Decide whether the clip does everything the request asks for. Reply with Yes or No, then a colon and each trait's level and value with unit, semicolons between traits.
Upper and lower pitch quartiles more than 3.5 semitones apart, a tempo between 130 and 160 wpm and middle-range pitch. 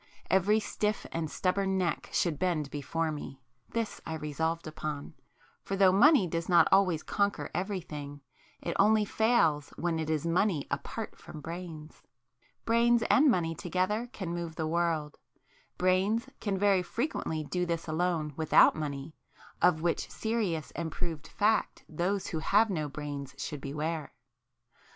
Yes: average, 4.1 semitones; average, 140 wpm; medium, 170 Hz